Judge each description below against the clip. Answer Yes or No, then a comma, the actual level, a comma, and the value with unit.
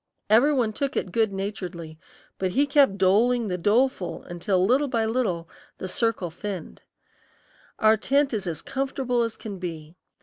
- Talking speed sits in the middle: Yes, average, 160 wpm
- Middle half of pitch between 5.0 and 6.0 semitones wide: Yes, wide, 5.4 semitones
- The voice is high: Yes, high, 215 Hz